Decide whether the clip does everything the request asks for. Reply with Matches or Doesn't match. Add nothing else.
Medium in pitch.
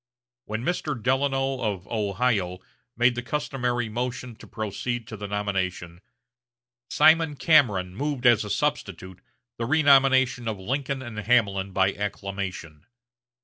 Doesn't match